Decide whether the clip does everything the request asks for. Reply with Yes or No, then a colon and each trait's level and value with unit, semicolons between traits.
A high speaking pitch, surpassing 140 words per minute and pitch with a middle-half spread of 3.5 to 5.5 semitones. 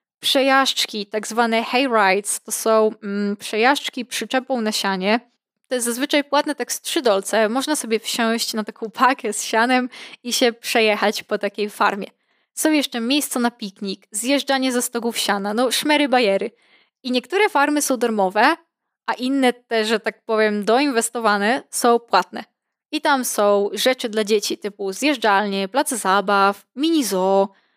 Yes: high, 235 Hz; average, 155 wpm; average, 3.9 semitones